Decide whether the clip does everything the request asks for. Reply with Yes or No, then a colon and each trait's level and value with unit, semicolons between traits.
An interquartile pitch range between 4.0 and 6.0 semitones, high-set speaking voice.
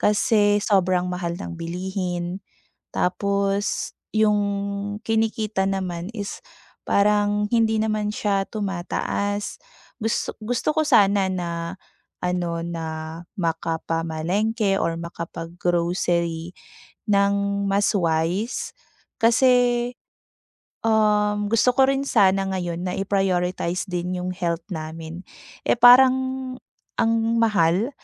No: average, 3.4 semitones; high, 195 Hz